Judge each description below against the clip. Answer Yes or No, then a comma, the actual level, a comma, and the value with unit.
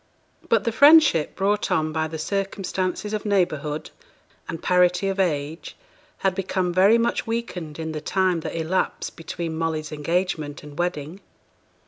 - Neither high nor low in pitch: Yes, medium, 175 Hz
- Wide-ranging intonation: No, average, 3.5 semitones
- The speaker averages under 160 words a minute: Yes, average, 145 wpm